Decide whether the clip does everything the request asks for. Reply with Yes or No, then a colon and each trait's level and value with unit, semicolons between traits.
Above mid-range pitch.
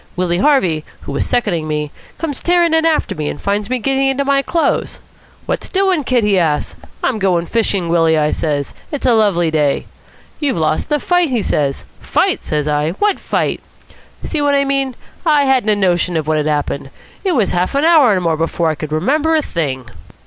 Yes: high, 205 Hz